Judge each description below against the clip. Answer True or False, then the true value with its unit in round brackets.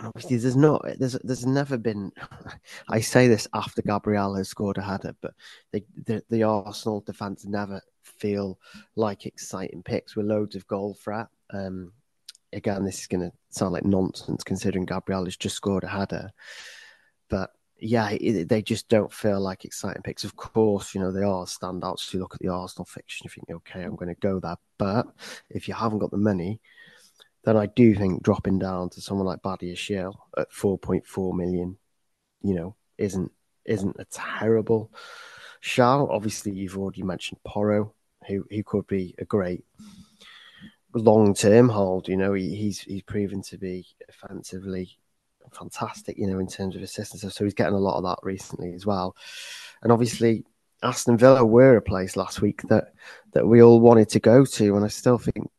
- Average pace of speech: True (185 wpm)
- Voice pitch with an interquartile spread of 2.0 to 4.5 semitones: True (2.6 semitones)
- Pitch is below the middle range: True (100 Hz)